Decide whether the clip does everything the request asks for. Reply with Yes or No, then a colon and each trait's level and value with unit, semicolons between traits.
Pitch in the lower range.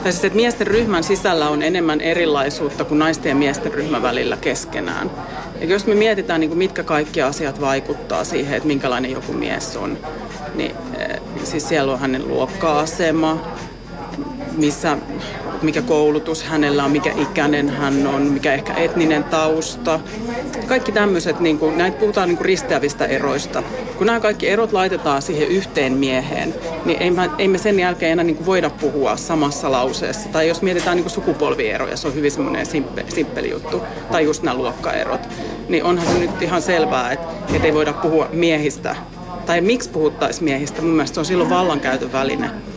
No: medium, 160 Hz